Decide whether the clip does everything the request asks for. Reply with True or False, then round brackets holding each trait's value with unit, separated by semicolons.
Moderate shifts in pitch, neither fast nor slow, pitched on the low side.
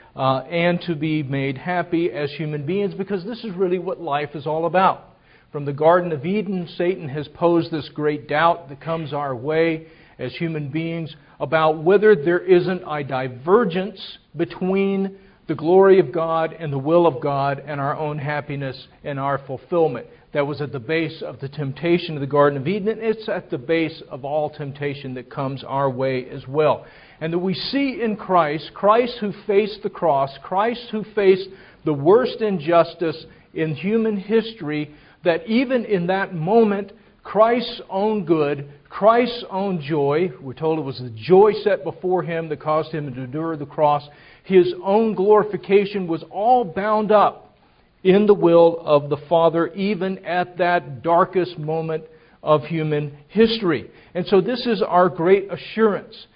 False (4.5 semitones; 170 wpm; 165 Hz)